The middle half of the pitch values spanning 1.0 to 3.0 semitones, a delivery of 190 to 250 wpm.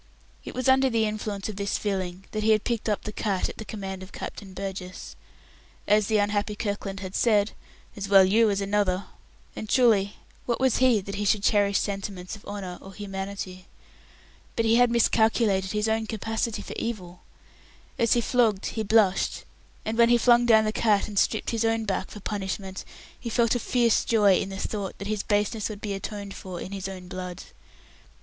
Yes: narrow, 2.4 semitones; average, 200 wpm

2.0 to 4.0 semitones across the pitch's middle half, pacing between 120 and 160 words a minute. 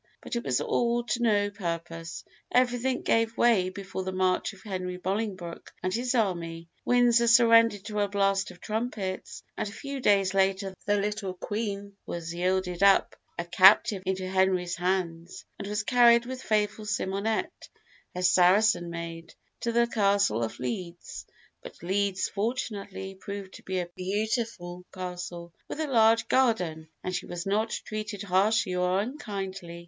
Yes: average, 3.4 semitones; average, 155 wpm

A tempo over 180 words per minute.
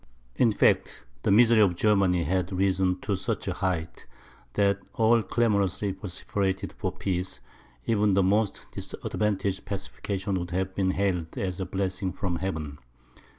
No: average, 150 wpm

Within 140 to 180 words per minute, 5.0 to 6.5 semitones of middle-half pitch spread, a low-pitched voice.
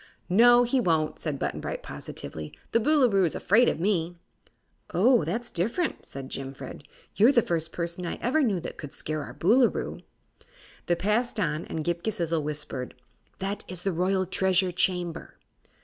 No: average, 160 wpm; wide, 5.4 semitones; medium, 180 Hz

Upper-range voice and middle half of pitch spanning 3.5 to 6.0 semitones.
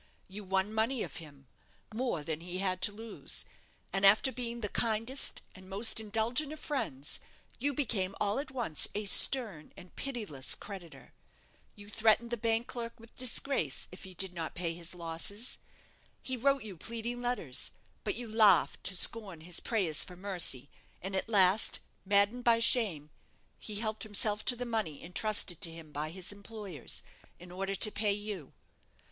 Yes: high, 205 Hz; average, 4.4 semitones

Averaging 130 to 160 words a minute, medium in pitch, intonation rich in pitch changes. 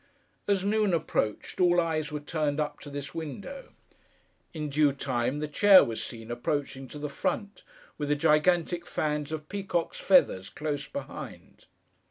No: average, 155 wpm; medium, 150 Hz; average, 3.4 semitones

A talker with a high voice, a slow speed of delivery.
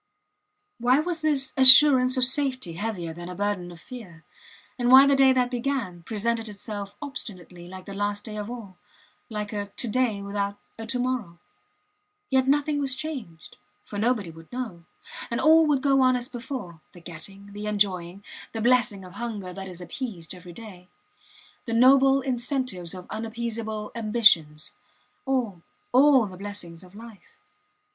No: high, 220 Hz; average, 160 wpm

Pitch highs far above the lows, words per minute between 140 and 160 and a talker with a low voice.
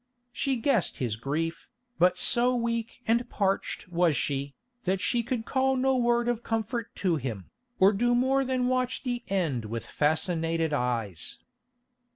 No: wide, 7.5 semitones; average, 155 wpm; high, 200 Hz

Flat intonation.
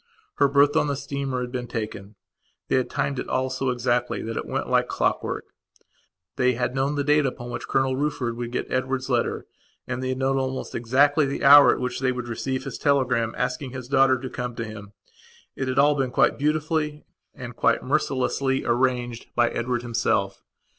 Yes: narrow, 2.1 semitones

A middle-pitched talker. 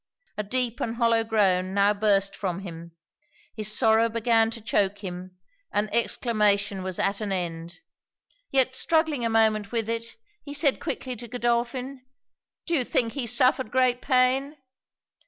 No: high, 225 Hz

